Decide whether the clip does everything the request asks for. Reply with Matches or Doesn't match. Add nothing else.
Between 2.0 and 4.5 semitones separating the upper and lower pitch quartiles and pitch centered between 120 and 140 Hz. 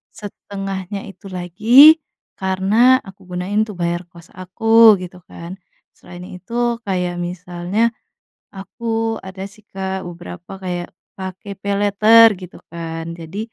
Doesn't match